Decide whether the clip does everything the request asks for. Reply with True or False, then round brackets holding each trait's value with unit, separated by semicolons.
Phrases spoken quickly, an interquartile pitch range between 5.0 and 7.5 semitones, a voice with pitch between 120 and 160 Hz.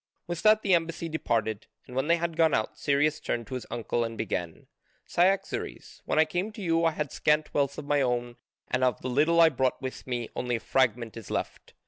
True (220 wpm; 5.3 semitones; 140 Hz)